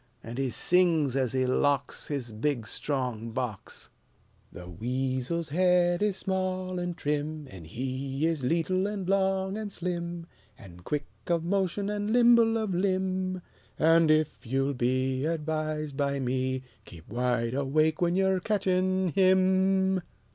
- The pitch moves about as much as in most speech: No, wide, 6.1 semitones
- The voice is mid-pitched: Yes, medium, 160 Hz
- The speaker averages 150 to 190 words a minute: No, average, 140 wpm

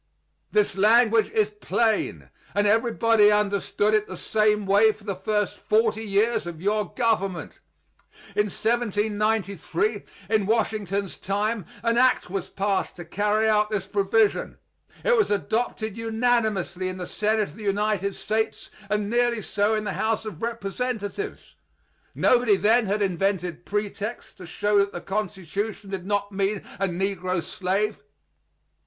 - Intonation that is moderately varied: No, narrow, 2.0 semitones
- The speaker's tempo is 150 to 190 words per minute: No, average, 140 wpm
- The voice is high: Yes, high, 210 Hz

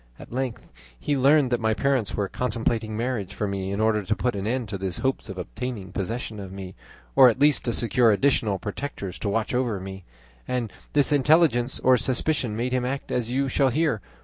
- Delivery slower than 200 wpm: No, fast, 205 wpm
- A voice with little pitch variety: No, average, 4.1 semitones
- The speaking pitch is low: Yes, low, 120 Hz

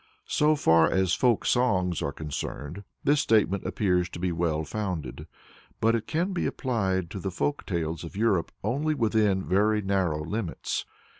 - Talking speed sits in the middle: Yes, average, 160 wpm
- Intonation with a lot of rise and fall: No, average, 4.8 semitones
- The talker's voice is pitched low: Yes, very low, 95 Hz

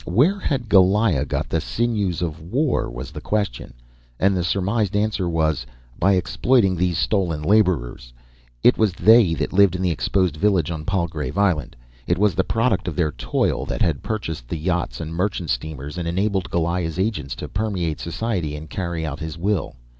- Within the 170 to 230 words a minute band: Yes, average, 180 wpm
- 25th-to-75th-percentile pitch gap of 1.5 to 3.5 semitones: No, average, 4.4 semitones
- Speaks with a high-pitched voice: No, very low, 90 Hz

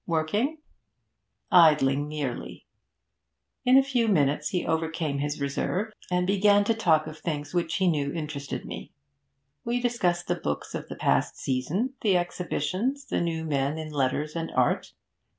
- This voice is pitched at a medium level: Yes, medium, 165 Hz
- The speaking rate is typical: Yes, average, 155 wpm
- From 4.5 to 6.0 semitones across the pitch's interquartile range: Yes, average, 5.1 semitones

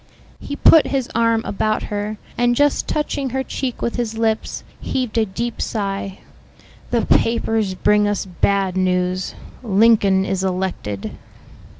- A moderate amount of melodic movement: Yes, average, 3.6 semitones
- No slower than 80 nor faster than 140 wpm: Yes, slow, 135 wpm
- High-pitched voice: Yes, high, 215 Hz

